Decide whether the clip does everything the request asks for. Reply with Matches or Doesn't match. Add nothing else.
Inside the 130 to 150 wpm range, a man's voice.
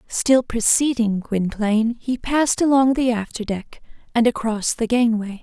Doesn't match